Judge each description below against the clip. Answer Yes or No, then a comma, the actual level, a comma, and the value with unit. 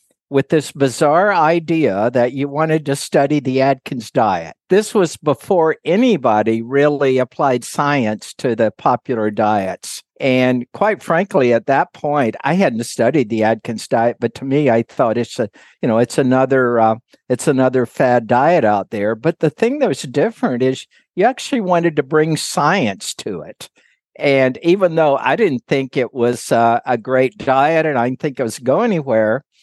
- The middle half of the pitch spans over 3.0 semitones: Yes, average, 4.5 semitones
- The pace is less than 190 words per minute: Yes, average, 180 wpm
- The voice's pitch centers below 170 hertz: Yes, low, 135 Hz